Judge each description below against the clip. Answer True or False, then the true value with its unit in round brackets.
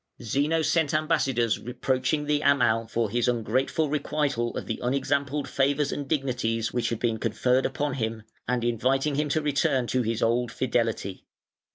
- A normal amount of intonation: True (3.4 semitones)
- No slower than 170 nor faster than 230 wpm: False (160 wpm)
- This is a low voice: True (130 Hz)